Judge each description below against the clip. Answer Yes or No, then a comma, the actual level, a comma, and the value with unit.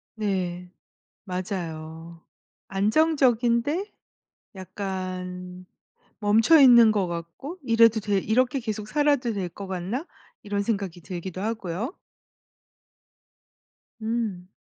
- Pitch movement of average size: Yes, average, 4.4 semitones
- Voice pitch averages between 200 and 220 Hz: Yes, high, 205 Hz